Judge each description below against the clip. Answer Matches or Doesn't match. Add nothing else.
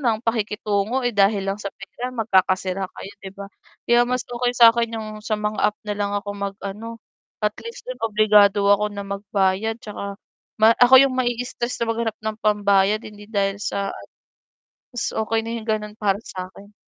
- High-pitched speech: Matches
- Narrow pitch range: Matches